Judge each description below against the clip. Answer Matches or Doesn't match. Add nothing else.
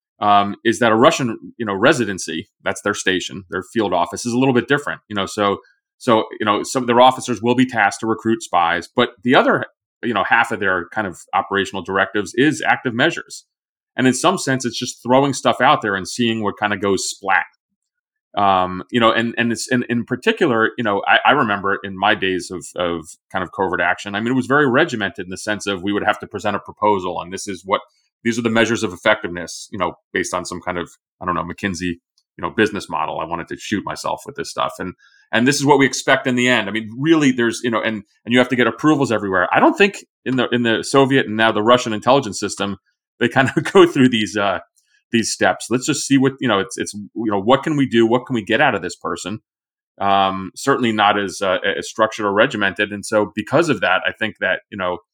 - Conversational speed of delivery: Doesn't match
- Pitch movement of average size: Matches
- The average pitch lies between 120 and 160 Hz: Doesn't match